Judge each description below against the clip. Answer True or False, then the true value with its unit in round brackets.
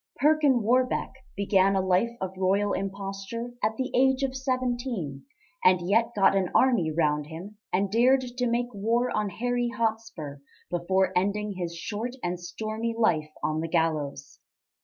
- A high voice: True (205 Hz)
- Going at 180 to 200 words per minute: False (155 wpm)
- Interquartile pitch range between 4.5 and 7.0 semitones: True (5.1 semitones)